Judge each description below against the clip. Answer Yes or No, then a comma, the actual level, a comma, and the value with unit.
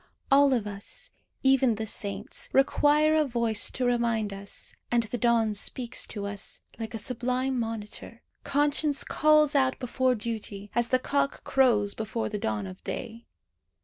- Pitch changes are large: No, average, 3.8 semitones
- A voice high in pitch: Yes, high, 235 Hz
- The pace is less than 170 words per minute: Yes, average, 155 wpm